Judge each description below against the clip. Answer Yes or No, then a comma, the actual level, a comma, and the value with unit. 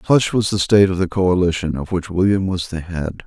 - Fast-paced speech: Yes, fast, 240 wpm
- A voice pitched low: Yes, very low, 90 Hz